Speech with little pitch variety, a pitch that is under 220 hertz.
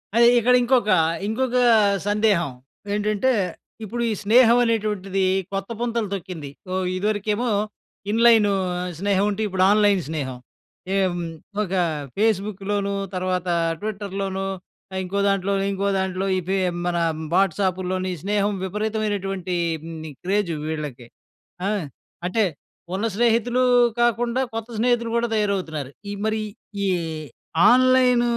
No: average, 3.2 semitones; high, 205 Hz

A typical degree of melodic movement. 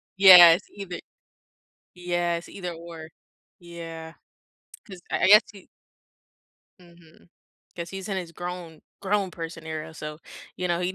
No: narrow, 1.8 semitones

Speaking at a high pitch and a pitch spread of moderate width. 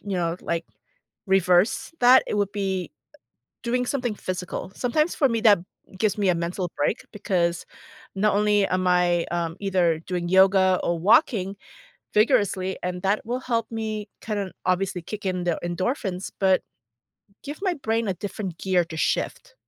Yes: high, 195 Hz; average, 3.5 semitones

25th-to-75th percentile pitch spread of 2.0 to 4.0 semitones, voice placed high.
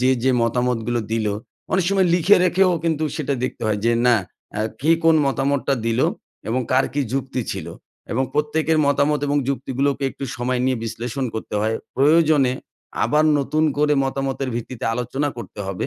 No: average, 3.5 semitones; low, 135 Hz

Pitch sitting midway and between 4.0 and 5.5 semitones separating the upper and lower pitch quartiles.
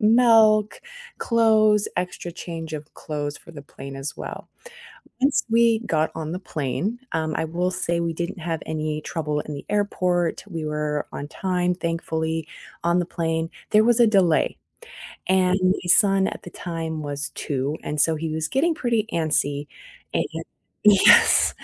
Yes: medium, 170 Hz; average, 4.4 semitones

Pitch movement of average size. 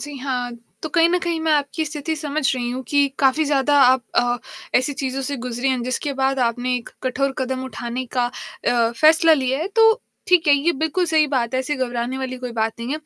Yes: average, 3.3 semitones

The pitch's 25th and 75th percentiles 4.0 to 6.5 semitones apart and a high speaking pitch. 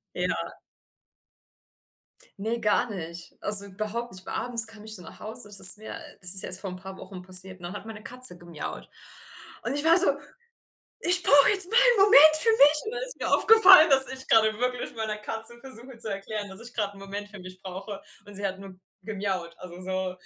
Yes: average, 4.9 semitones; high, 210 Hz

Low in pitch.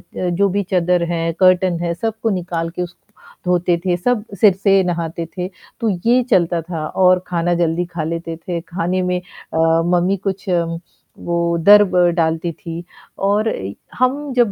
No: medium, 180 Hz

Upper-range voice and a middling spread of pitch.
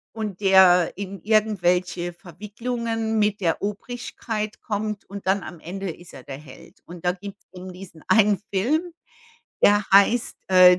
Yes: high, 195 Hz; average, 3.1 semitones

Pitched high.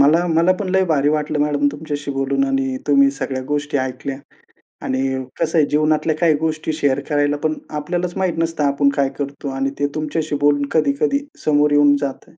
No: medium, 145 Hz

